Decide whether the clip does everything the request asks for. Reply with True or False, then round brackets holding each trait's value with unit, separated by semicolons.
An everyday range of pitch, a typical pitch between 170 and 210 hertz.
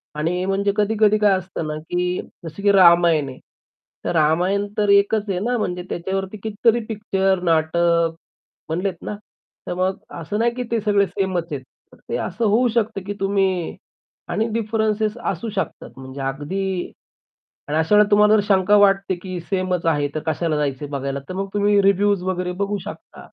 True (3.3 semitones; 190 Hz)